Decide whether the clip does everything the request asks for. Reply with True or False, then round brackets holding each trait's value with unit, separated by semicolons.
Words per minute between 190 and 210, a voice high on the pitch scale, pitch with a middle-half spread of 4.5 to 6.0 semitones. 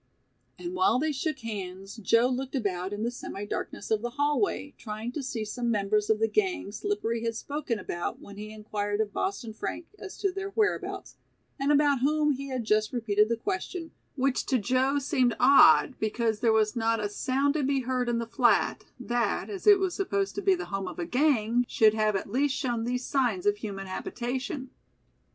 True (200 wpm; 245 Hz; 5.0 semitones)